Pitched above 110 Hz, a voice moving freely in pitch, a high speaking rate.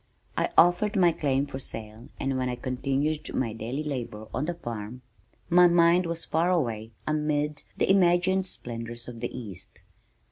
No: medium, 140 Hz; wide, 6.3 semitones; average, 165 wpm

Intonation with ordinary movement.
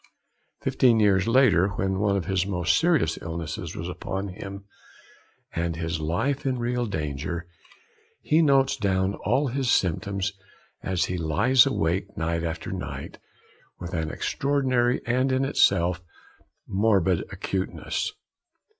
No: wide, 6.3 semitones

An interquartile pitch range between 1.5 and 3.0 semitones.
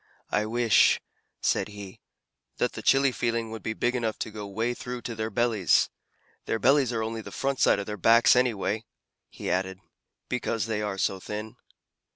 Yes: narrow, 2.4 semitones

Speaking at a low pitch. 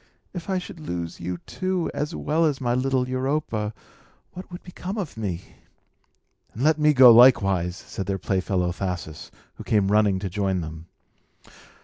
Yes: low, 110 Hz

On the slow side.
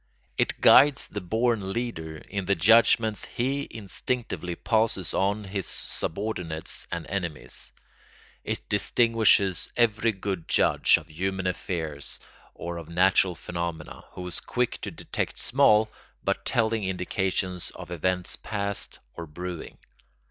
Yes: slow, 125 wpm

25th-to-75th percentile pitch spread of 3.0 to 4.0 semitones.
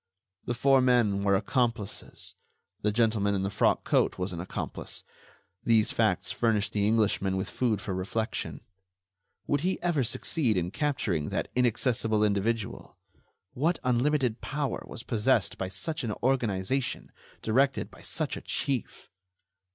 No: average, 4.4 semitones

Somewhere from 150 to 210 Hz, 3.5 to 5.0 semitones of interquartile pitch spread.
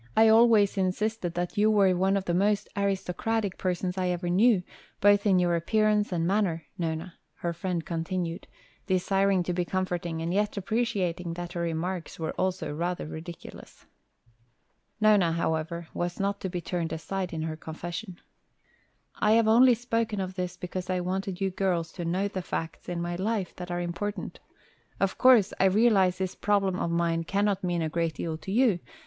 No: medium, 185 Hz; average, 2.8 semitones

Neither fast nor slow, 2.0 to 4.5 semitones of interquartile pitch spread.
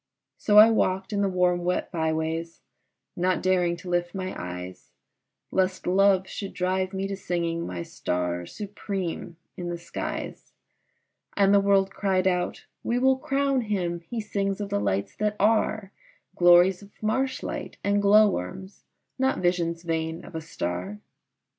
Yes: average, 155 wpm; average, 3.1 semitones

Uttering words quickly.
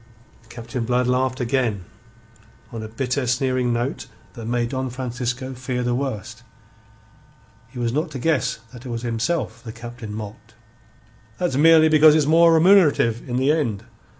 No: average, 155 wpm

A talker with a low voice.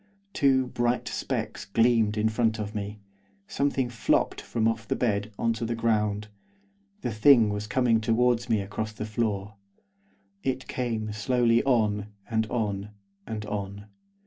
Yes: low, 110 Hz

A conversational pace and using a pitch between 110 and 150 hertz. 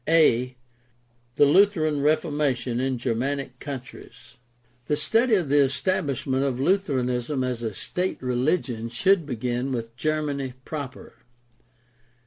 No: slow, 115 wpm; low, 135 Hz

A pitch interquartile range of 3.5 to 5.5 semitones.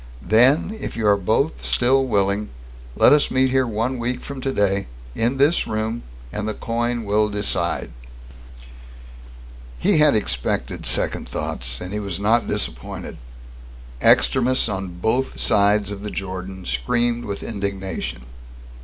Yes: average, 3.8 semitones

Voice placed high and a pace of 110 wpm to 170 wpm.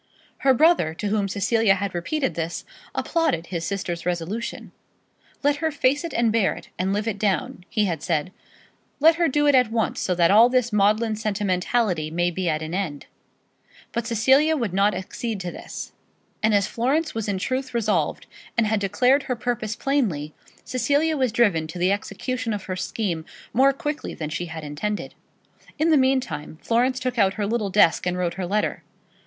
No: high, 210 Hz; average, 185 wpm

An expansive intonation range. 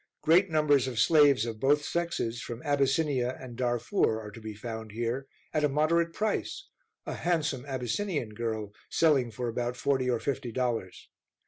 No: average, 4.4 semitones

